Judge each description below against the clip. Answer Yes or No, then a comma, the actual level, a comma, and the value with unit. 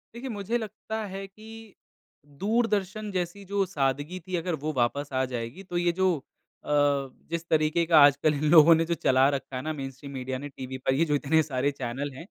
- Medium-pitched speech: Yes, medium, 160 Hz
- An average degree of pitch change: No, wide, 5.8 semitones